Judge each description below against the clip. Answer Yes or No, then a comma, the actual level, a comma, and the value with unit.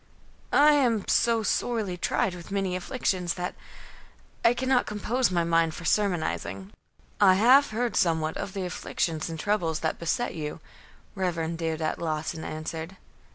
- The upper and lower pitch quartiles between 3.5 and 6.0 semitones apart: Yes, average, 4.8 semitones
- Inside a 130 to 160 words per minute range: Yes, average, 150 wpm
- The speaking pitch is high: No, medium, 180 Hz